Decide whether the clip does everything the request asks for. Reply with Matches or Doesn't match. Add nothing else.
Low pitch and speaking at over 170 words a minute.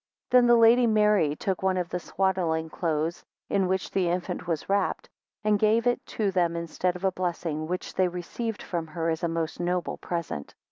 Doesn't match